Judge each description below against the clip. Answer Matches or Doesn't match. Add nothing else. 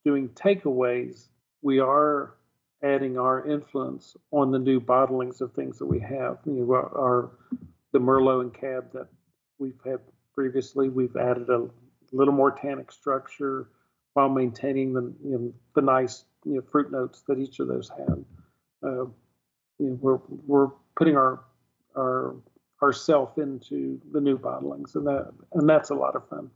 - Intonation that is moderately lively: Doesn't match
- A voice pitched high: Doesn't match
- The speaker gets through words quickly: Doesn't match